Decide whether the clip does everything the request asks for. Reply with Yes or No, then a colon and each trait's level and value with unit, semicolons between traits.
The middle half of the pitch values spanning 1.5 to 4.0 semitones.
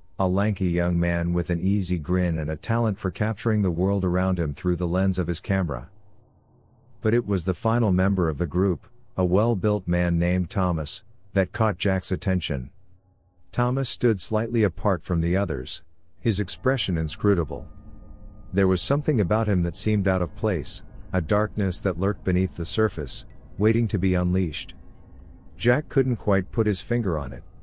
Yes: average, 3.3 semitones